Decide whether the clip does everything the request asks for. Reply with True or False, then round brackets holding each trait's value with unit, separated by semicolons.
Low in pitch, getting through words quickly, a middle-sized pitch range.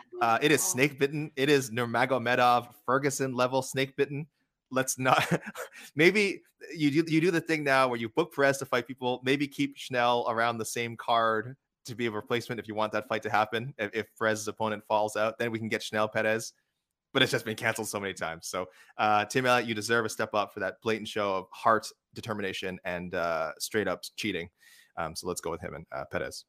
True (120 Hz; 220 wpm; 3.6 semitones)